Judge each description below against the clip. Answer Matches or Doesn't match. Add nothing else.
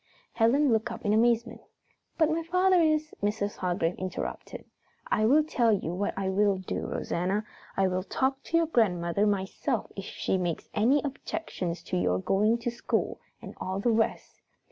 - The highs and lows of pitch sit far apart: Matches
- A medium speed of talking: Matches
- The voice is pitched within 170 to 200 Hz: Doesn't match